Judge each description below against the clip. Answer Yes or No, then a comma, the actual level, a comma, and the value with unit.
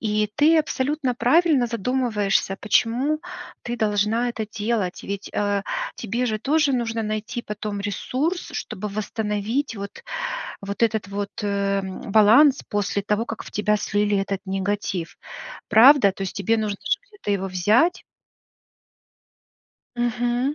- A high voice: Yes, high, 215 Hz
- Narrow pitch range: No, average, 3.4 semitones